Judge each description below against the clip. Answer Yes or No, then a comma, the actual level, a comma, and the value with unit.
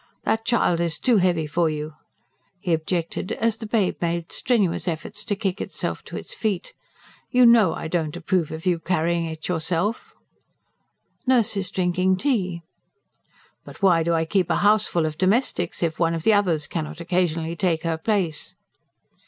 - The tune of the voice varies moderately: Yes, average, 3.8 semitones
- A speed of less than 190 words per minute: Yes, average, 170 wpm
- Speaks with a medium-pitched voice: Yes, medium, 175 Hz